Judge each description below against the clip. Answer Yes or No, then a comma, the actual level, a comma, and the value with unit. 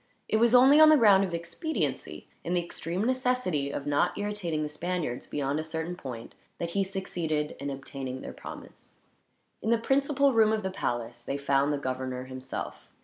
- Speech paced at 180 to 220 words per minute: Yes, average, 185 wpm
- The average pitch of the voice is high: No, medium, 170 Hz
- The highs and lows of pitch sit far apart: Yes, wide, 7.7 semitones